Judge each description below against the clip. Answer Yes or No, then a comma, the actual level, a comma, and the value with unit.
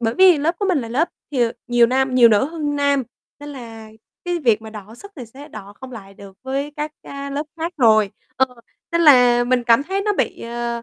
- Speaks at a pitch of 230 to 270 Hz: Yes, very high, 260 Hz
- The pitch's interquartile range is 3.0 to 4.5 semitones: Yes, average, 4.2 semitones